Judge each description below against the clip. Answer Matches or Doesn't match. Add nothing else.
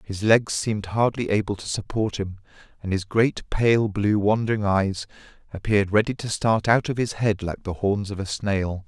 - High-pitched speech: Doesn't match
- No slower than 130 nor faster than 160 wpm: Doesn't match